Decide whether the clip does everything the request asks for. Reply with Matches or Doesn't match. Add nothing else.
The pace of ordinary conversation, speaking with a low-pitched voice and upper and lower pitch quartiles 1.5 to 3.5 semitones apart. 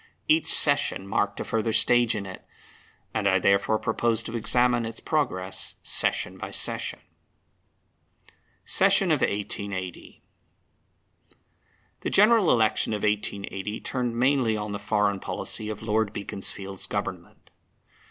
Doesn't match